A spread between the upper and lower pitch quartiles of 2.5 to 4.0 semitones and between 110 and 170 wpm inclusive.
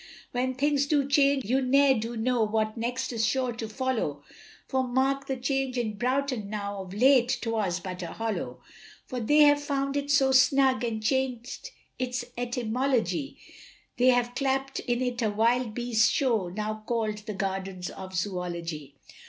Yes: average, 3.6 semitones; average, 165 wpm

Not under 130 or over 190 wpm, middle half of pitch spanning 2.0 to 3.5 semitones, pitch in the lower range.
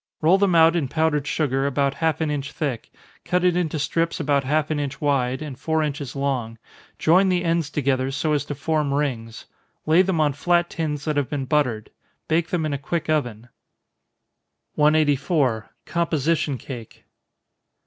No: average, 170 wpm; average, 2.9 semitones; medium, 150 Hz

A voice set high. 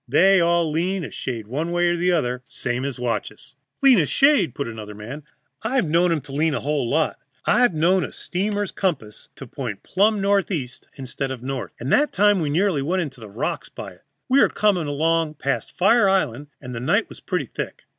No: medium, 160 Hz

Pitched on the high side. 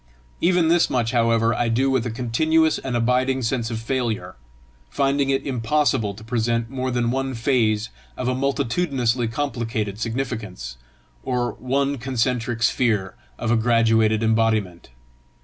No: low, 120 Hz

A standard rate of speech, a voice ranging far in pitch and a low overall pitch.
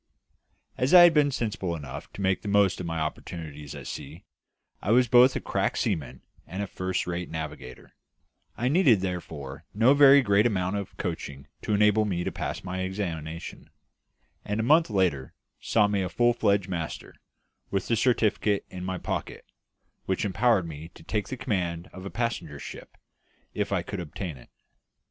No: average, 175 wpm; average, 4.8 semitones; very low, 95 Hz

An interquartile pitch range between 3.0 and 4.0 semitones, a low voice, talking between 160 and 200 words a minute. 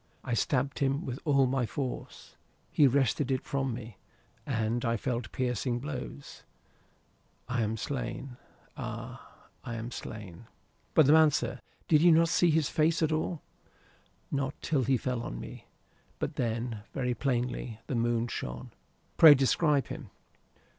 No: average, 3.3 semitones; low, 130 Hz; average, 150 wpm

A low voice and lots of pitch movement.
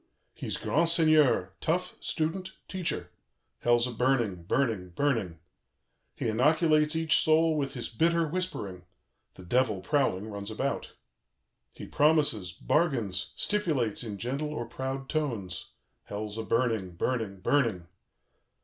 Yes: low, 130 Hz; wide, 6.9 semitones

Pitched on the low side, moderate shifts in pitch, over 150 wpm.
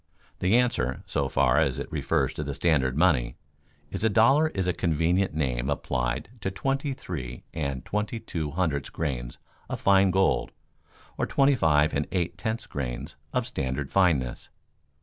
No: very low, 80 Hz; wide, 6.3 semitones; average, 160 wpm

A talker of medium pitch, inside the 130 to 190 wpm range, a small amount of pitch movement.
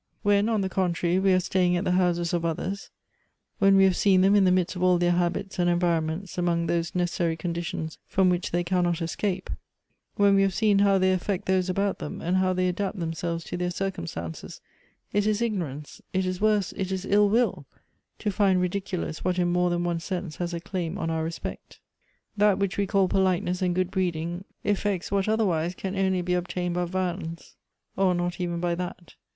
No: medium, 180 Hz; fast, 205 wpm; narrow, 2.0 semitones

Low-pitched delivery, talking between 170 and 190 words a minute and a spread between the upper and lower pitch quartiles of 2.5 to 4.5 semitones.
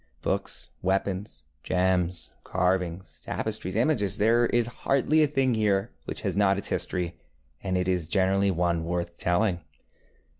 No: very low, 95 Hz; slow, 135 wpm; average, 3.3 semitones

